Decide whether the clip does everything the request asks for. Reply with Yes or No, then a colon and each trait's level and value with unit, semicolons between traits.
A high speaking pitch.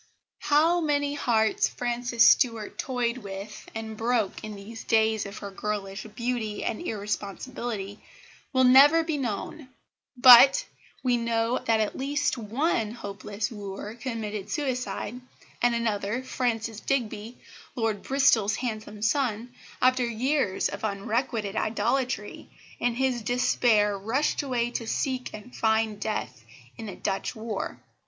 Yes: high, 230 Hz